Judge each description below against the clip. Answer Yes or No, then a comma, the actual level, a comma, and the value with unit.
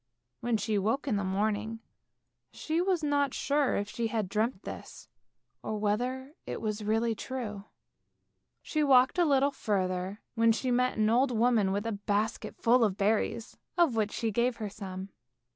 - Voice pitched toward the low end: No, high, 225 Hz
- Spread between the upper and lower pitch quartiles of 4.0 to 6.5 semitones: No, average, 3.6 semitones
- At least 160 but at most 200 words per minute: Yes, average, 170 wpm